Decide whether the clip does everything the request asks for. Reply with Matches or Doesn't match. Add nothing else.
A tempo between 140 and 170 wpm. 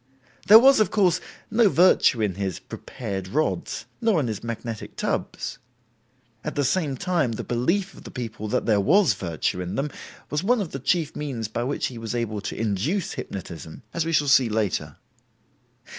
Doesn't match